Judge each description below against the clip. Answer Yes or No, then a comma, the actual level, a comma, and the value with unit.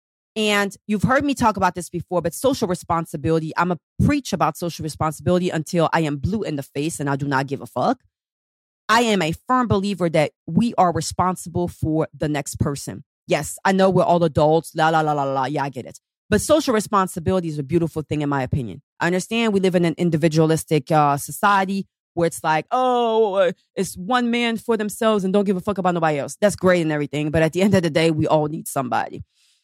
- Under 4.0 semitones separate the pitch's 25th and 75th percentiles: No, average, 4.3 semitones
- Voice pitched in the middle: Yes, medium, 170 Hz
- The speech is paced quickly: Yes, fast, 220 wpm